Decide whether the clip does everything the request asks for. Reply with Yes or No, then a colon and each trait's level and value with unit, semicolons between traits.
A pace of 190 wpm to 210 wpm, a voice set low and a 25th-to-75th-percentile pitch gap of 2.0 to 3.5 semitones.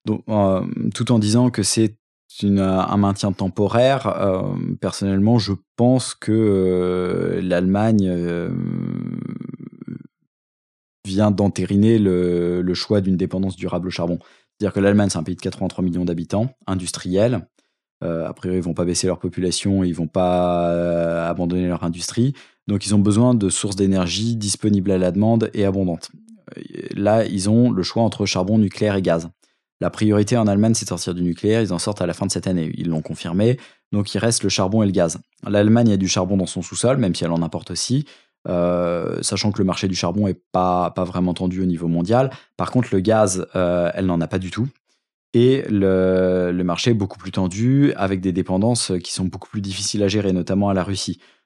Yes: average, 200 wpm; very low, 95 Hz; average, 2.9 semitones